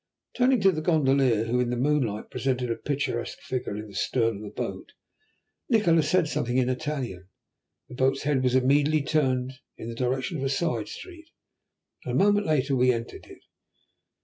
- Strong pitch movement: No, average, 3.8 semitones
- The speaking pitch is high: No, low, 130 Hz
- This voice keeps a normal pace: Yes, average, 180 wpm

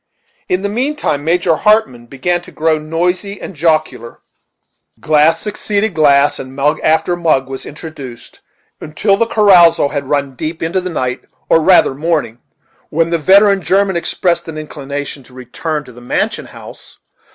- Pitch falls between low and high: Yes, medium, 160 Hz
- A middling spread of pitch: Yes, average, 4.2 semitones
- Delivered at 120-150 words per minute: No, average, 160 wpm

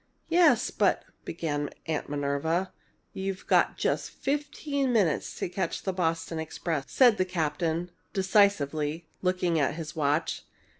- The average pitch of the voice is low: No, medium, 170 Hz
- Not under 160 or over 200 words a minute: No, slow, 135 wpm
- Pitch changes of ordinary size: Yes, average, 3.7 semitones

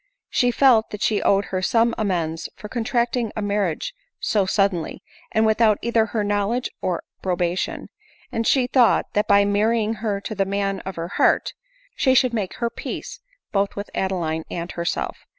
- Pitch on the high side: Yes, high, 205 Hz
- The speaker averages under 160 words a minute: No, average, 180 wpm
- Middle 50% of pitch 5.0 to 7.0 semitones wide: No, average, 3.2 semitones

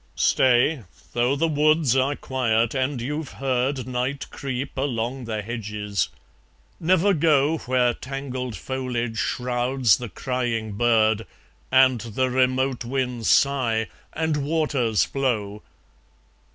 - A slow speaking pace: Yes, slow, 110 wpm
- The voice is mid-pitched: No, low, 130 Hz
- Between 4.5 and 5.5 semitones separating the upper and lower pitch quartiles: No, average, 2.8 semitones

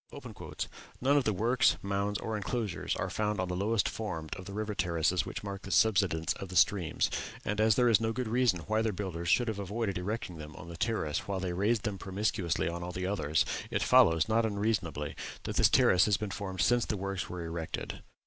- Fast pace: Yes, fast, 215 wpm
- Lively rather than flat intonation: No, average, 3.5 semitones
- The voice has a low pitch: Yes, low, 100 Hz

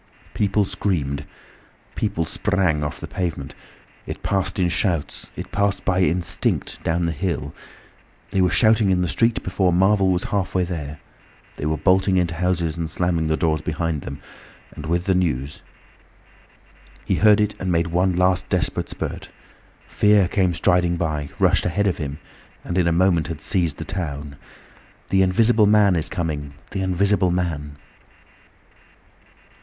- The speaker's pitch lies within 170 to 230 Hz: No, very low, 90 Hz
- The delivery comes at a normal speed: Yes, average, 155 wpm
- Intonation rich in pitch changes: No, average, 2.9 semitones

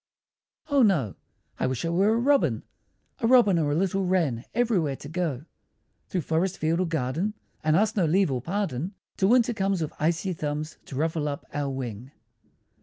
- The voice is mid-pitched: Yes, medium, 170 Hz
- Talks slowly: No, average, 180 wpm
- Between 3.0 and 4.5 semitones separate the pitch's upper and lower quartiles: No, average, 5.0 semitones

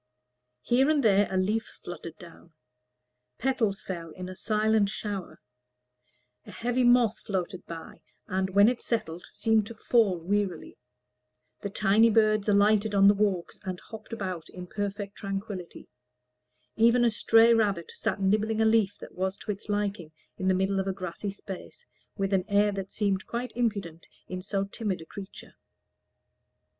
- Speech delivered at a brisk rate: No, average, 160 wpm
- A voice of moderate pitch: No, high, 200 Hz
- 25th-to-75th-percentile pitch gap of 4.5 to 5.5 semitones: No, narrow, 2.6 semitones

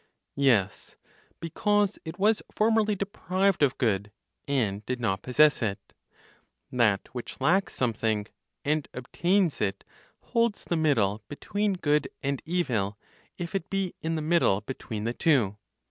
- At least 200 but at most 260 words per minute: No, slow, 135 wpm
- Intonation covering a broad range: Yes, wide, 8.7 semitones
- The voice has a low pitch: No, medium, 145 Hz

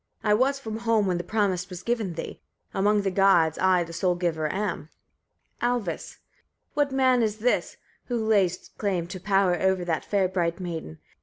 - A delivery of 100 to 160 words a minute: No, average, 180 wpm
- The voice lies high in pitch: Yes, high, 195 Hz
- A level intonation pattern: No, average, 3.7 semitones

